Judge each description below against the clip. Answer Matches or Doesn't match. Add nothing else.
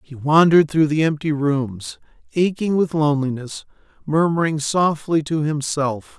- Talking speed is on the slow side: Matches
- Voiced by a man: Matches